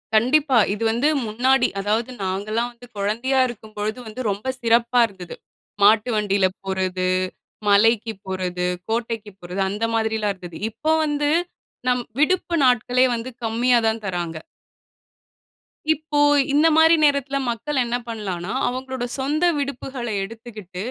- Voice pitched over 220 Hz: Yes, high, 230 Hz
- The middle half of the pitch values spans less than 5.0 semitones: Yes, average, 4.1 semitones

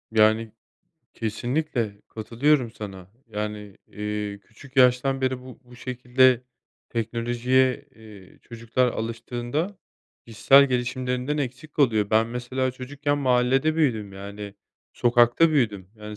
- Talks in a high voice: No, low, 120 Hz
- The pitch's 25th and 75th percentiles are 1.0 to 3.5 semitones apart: Yes, average, 3.1 semitones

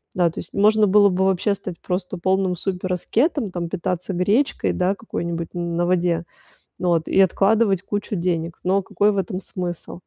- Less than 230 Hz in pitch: Yes, medium, 185 Hz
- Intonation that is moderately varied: No, narrow, 2.3 semitones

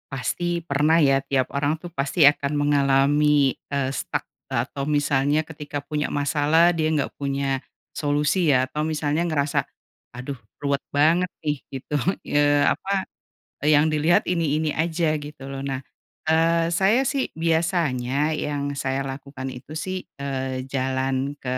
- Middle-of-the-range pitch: Yes, medium, 145 Hz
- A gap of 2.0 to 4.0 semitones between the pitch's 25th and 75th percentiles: Yes, narrow, 2.4 semitones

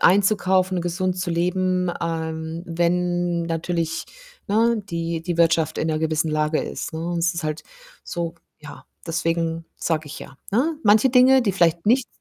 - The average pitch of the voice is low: No, medium, 170 Hz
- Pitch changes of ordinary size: No, narrow, 2.3 semitones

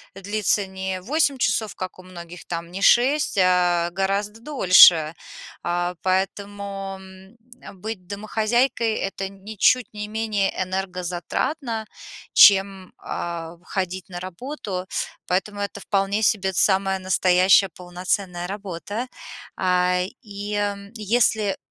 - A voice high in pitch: Yes, high, 195 Hz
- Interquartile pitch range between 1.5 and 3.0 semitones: Yes, narrow, 2.5 semitones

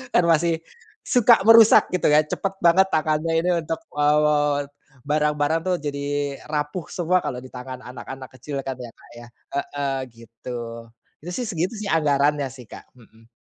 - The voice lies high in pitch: No, medium, 150 Hz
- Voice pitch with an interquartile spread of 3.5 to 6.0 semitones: Yes, average, 3.9 semitones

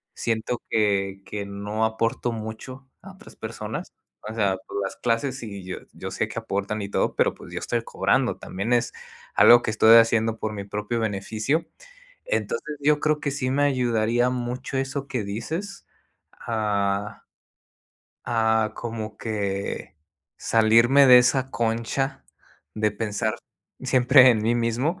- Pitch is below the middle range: Yes, low, 115 Hz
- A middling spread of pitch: Yes, average, 3.1 semitones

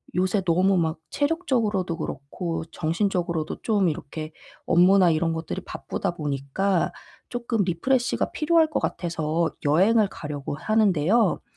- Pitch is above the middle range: No, medium, 180 Hz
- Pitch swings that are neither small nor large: Yes, average, 4.8 semitones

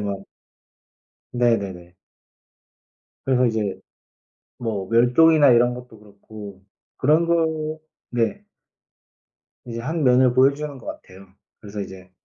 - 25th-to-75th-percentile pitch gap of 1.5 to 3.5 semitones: No, average, 5.2 semitones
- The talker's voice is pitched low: Yes, low, 120 Hz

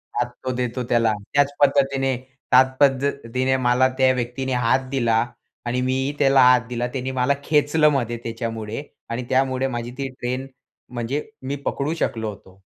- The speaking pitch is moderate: No, low, 130 Hz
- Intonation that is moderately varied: No, narrow, 2.1 semitones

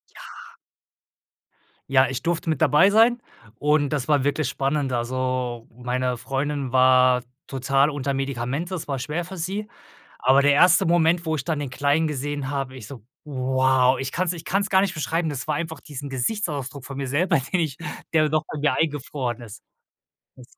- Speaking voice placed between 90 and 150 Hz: Yes, medium, 140 Hz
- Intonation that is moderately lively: Yes, average, 3.5 semitones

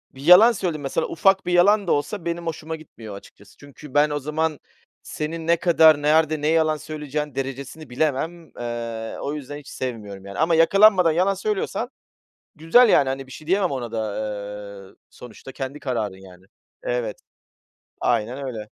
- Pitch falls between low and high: Yes, medium, 150 Hz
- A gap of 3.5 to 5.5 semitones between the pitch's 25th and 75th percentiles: Yes, average, 4.4 semitones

